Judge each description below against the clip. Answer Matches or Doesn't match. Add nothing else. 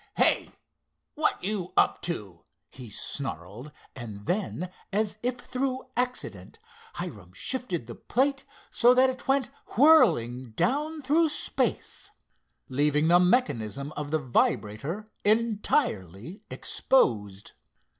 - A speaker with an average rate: Doesn't match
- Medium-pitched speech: Matches